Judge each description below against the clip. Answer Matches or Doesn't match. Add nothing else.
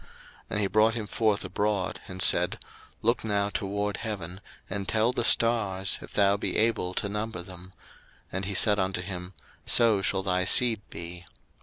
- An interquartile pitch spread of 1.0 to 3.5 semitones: Matches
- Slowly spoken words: Doesn't match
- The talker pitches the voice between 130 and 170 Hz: Doesn't match